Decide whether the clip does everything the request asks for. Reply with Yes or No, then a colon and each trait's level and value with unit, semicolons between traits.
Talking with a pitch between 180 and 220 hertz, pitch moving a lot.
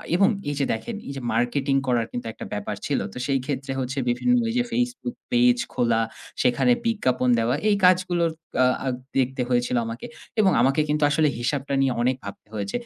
No: low, 135 Hz; wide, 6.8 semitones